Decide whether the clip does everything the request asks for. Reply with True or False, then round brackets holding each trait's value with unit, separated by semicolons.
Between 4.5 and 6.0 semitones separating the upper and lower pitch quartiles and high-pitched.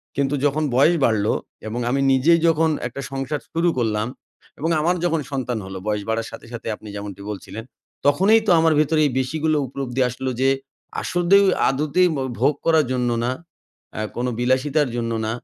False (4.9 semitones; 135 Hz)